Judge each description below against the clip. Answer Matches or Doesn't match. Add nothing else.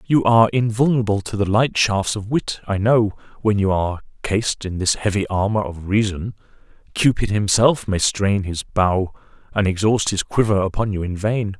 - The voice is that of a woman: Doesn't match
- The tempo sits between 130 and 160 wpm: Doesn't match